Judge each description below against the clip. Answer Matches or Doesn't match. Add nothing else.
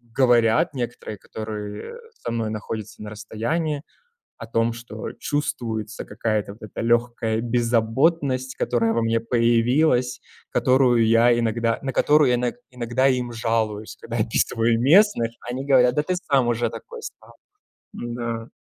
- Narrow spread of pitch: Matches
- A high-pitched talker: Doesn't match